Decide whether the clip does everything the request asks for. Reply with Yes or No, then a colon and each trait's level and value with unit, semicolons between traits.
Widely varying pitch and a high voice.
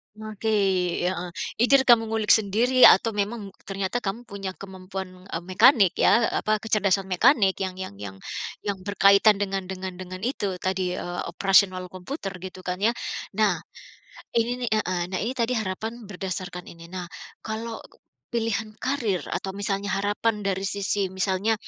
No: average, 2.9 semitones; high, 200 Hz